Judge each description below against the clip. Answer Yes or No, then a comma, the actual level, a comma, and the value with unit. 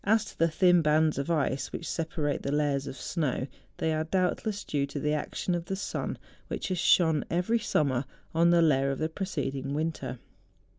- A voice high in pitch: No, medium, 155 Hz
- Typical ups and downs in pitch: Yes, average, 3.6 semitones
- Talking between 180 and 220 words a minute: Yes, average, 190 wpm